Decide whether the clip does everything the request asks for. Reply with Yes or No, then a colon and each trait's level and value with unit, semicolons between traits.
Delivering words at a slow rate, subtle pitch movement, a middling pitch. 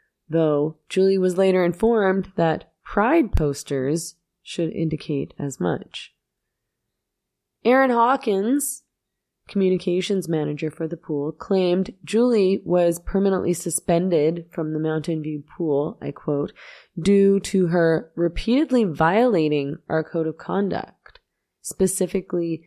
No: slow, 110 wpm; average, 3.6 semitones; medium, 175 Hz